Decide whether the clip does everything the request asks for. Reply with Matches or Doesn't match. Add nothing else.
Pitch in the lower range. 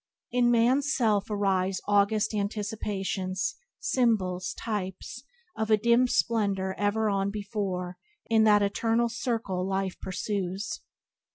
Doesn't match